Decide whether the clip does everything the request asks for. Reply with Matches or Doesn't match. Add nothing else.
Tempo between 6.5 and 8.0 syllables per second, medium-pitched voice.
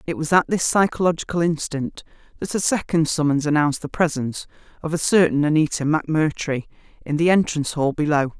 Matches